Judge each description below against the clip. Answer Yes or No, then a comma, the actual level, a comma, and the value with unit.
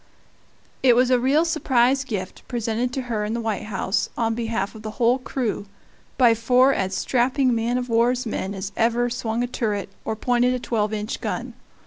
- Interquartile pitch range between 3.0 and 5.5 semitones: No, narrow, 2.5 semitones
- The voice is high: Yes, high, 235 Hz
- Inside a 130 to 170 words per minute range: No, average, 190 wpm